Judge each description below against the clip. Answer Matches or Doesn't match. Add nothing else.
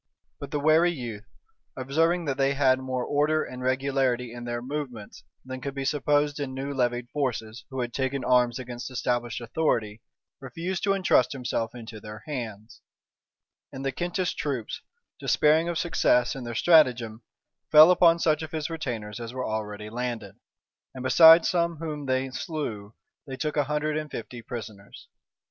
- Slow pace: Doesn't match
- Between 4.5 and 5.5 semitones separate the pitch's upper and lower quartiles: Doesn't match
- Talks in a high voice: Doesn't match